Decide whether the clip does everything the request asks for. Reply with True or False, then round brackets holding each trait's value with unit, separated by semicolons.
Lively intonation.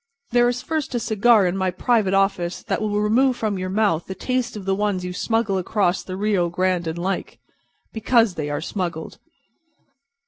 False (3.5 semitones)